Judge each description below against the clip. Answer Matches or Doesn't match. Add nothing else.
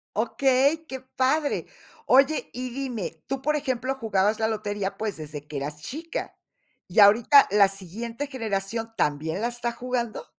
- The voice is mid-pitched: Doesn't match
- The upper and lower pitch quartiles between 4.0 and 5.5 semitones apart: Matches